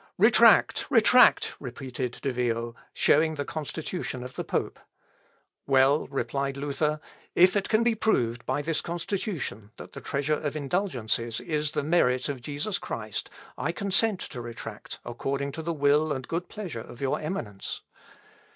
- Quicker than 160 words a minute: No, average, 150 wpm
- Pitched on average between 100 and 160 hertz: Yes, medium, 140 Hz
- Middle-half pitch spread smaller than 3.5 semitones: No, average, 4.6 semitones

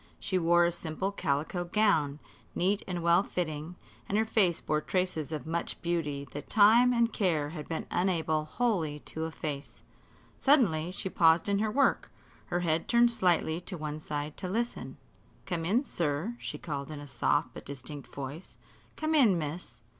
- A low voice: No, medium, 170 Hz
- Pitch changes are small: No, average, 4.4 semitones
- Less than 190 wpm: Yes, average, 170 wpm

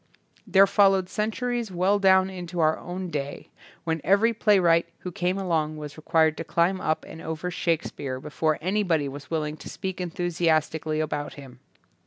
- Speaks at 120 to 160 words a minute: No, average, 175 wpm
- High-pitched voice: No, medium, 170 Hz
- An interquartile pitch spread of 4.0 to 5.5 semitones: No, average, 3.4 semitones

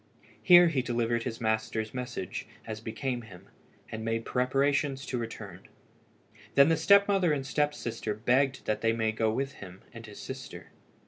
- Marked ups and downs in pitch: No, average, 3.8 semitones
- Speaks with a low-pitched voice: Yes, low, 120 Hz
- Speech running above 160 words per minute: Yes, average, 170 wpm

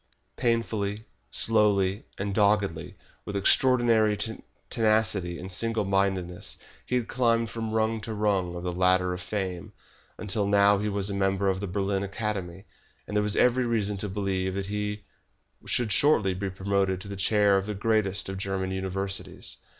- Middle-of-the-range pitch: No, low, 100 Hz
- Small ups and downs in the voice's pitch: Yes, narrow, 2.1 semitones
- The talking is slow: No, average, 165 wpm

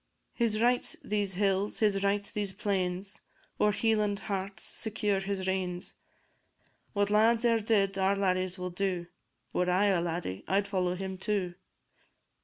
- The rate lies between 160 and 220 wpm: No, average, 145 wpm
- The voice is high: Yes, high, 195 Hz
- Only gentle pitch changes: Yes, narrow, 1.9 semitones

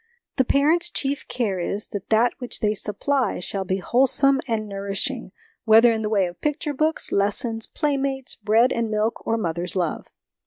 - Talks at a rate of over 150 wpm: Yes, average, 170 wpm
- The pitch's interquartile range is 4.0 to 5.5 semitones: Yes, average, 5.1 semitones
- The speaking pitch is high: Yes, high, 225 Hz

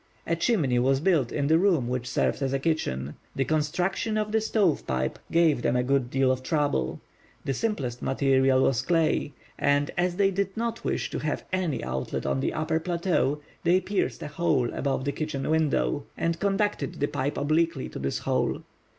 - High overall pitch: No, medium, 150 Hz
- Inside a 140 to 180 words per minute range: No, average, 190 wpm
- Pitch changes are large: No, average, 4.7 semitones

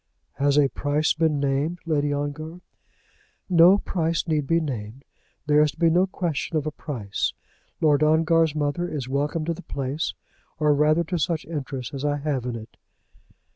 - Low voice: No, medium, 150 Hz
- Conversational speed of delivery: Yes, average, 175 wpm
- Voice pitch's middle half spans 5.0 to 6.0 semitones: No, narrow, 2.5 semitones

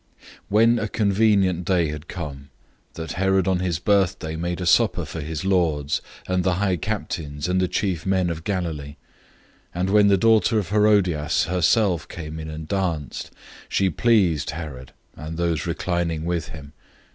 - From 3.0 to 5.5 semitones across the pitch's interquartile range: Yes, average, 3.3 semitones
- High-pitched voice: No, very low, 90 Hz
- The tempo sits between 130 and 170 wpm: Yes, average, 155 wpm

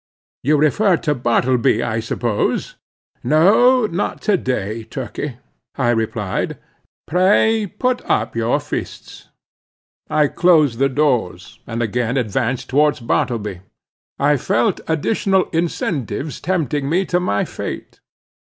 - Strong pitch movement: Yes, wide, 6.6 semitones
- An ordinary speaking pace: No, slow, 115 wpm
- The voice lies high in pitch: No, medium, 140 Hz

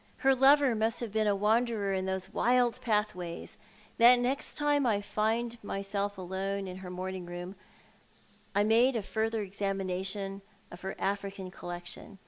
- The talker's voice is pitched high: Yes, high, 205 Hz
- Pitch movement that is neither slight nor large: Yes, average, 3.5 semitones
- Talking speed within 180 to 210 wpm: No, average, 150 wpm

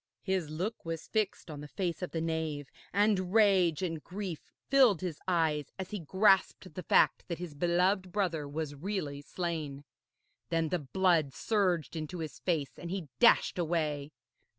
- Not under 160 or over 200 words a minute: Yes, average, 165 wpm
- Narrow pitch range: No, average, 3.5 semitones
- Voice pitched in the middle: Yes, medium, 170 Hz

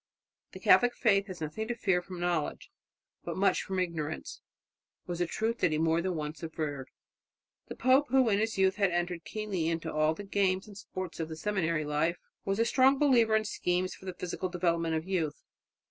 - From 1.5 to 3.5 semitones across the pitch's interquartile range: No, average, 4.1 semitones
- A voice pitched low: No, medium, 180 Hz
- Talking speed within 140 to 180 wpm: No, average, 200 wpm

